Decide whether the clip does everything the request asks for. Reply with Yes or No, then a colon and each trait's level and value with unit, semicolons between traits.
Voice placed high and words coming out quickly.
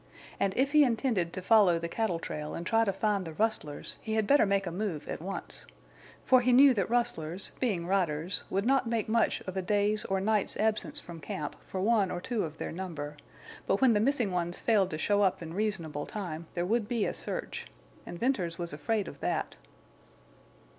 Yes: high, 195 Hz; fast, 210 wpm